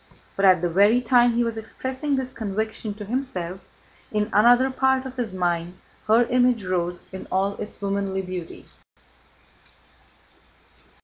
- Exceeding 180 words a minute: No, average, 140 wpm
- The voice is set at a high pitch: Yes, high, 215 Hz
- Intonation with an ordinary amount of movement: Yes, average, 4.6 semitones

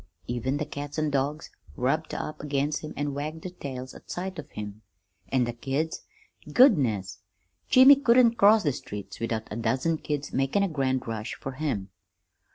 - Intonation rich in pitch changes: No, average, 4.4 semitones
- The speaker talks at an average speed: Yes, average, 170 wpm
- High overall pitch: No, medium, 140 Hz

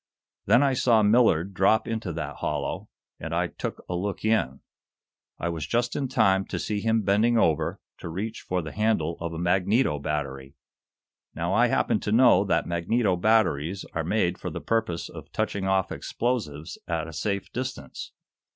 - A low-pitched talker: Yes, very low, 95 Hz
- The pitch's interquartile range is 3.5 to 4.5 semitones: No, average, 5.1 semitones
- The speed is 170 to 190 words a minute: Yes, average, 175 wpm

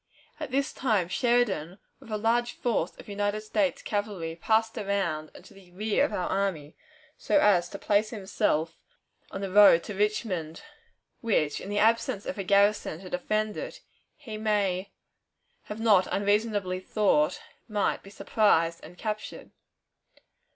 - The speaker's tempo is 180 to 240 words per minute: No, average, 150 wpm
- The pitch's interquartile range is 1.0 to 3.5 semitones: Yes, average, 3.0 semitones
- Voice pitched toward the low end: No, high, 205 Hz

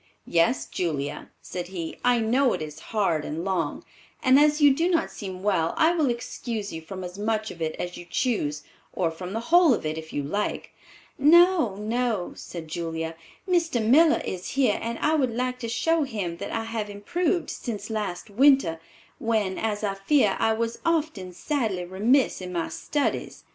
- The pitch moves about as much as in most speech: No, wide, 6.7 semitones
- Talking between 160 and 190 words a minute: Yes, average, 185 wpm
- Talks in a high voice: Yes, high, 215 Hz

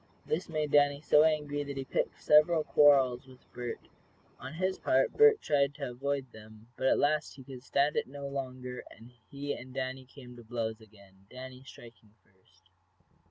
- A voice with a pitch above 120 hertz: Yes, low, 135 Hz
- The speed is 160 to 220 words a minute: Yes, average, 180 wpm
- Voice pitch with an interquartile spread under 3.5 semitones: Yes, average, 2.9 semitones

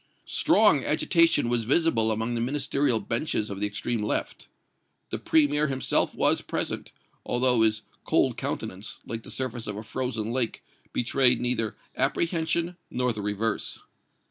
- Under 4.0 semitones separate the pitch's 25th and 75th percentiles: Yes, average, 3.4 semitones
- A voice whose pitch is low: Yes, low, 120 Hz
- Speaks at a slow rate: No, average, 145 wpm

